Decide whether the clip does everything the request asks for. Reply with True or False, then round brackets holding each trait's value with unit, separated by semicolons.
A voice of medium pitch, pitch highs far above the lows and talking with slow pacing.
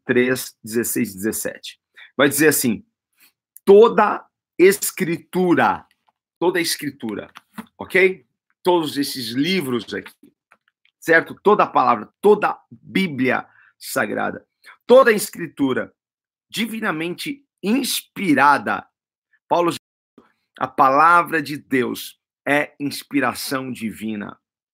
True (160 Hz; 8.3 semitones; 80 wpm)